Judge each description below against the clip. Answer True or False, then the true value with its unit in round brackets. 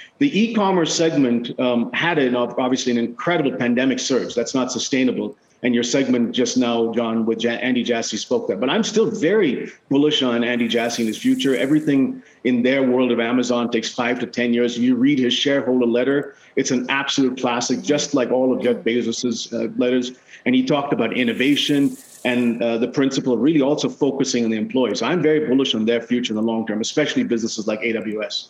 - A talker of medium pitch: False (125 Hz)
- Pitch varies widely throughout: False (2.7 semitones)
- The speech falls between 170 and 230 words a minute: True (205 wpm)